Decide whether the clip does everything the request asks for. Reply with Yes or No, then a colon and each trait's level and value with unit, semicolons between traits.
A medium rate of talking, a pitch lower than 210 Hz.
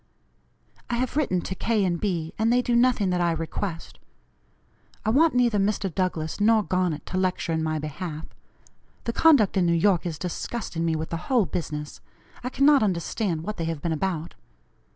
Yes: average, 185 wpm; medium, 185 Hz